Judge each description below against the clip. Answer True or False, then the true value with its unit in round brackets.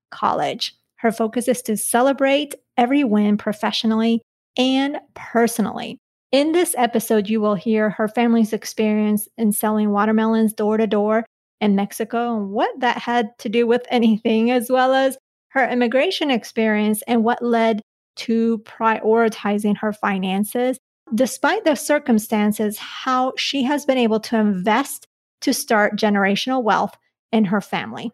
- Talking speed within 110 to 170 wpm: True (140 wpm)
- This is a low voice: False (230 Hz)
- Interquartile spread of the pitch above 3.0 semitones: False (2.7 semitones)